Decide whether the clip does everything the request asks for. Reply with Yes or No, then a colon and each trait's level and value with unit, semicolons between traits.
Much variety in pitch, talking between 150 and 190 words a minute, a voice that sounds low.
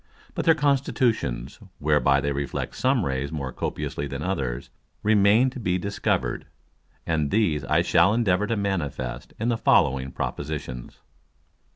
No: wide, 7.8 semitones; average, 140 wpm; very low, 80 Hz